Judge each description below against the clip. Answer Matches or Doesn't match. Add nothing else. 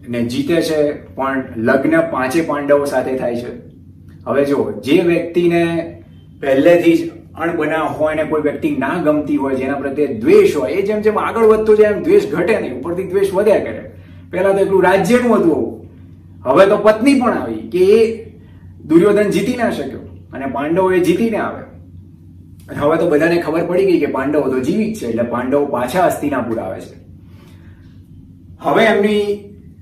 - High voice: Doesn't match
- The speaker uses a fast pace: Matches